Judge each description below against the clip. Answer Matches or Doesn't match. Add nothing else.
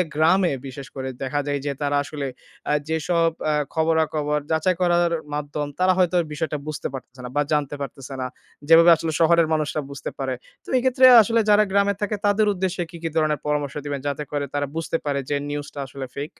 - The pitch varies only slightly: Doesn't match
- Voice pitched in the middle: Matches